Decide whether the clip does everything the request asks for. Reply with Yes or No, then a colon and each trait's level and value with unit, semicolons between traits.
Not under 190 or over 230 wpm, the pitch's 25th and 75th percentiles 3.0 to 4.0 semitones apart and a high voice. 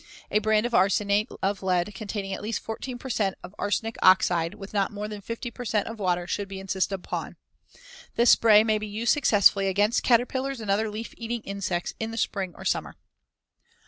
No: average, 200 wpm; narrow, 2.5 semitones; high, 210 Hz